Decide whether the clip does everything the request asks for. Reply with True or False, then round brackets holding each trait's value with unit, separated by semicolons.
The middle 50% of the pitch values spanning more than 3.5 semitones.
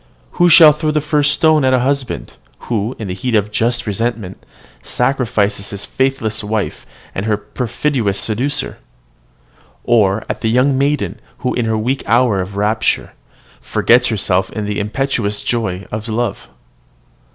True (4.2 semitones)